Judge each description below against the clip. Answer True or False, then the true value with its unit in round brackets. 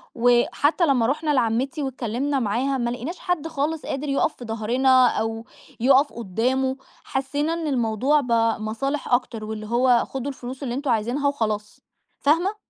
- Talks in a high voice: True (260 Hz)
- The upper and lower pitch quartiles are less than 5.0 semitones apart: True (3.5 semitones)